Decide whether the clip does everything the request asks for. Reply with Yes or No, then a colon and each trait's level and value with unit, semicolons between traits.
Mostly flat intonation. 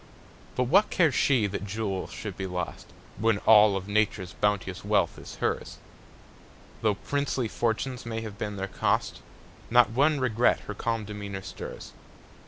No: average, 3.4 semitones